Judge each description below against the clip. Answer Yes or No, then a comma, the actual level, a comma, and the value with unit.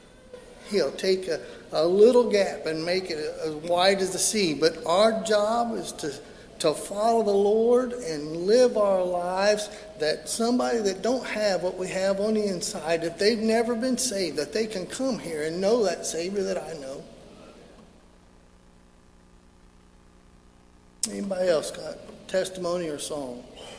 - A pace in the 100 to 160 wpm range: Yes, average, 155 wpm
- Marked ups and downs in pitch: Yes, wide, 5.7 semitones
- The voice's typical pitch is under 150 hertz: No, high, 190 Hz